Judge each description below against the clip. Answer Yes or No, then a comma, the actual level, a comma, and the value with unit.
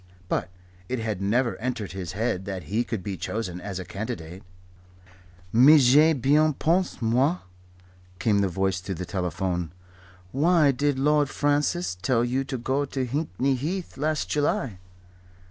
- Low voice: Yes, low, 120 Hz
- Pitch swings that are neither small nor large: No, wide, 7.1 semitones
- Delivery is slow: No, average, 155 wpm